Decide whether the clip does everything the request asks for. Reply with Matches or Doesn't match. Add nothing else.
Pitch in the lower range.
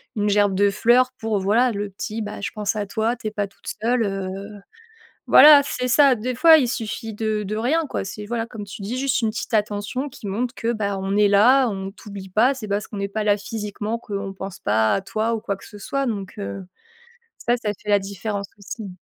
Doesn't match